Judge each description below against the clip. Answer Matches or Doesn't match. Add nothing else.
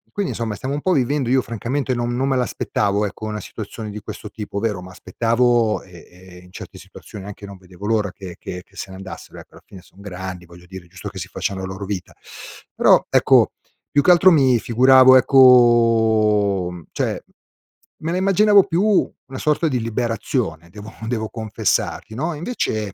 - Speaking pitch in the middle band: Doesn't match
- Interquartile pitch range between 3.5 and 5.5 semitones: Matches